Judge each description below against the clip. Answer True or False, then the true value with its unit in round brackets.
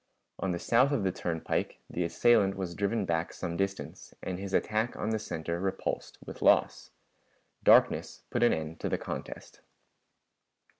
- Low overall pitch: True (95 Hz)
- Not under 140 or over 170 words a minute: True (160 wpm)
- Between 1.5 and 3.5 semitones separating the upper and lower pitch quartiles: False (3.9 semitones)